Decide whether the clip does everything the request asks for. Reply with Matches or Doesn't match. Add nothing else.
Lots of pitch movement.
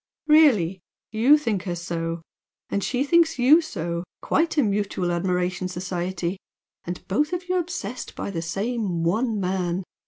Matches